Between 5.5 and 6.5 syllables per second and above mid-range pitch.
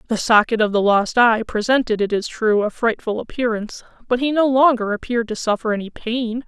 Yes: 5.6 syllables/s; high, 230 Hz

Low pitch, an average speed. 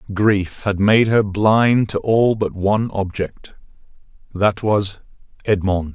No: low, 100 Hz; slow, 120 wpm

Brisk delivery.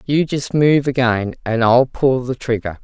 No: average, 190 wpm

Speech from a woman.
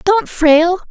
Yes: female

